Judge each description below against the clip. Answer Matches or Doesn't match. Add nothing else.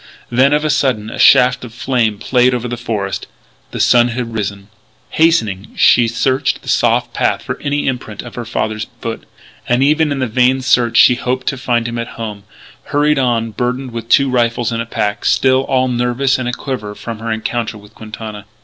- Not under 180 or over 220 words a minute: Matches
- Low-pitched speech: Matches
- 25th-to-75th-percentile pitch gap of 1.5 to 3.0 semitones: Matches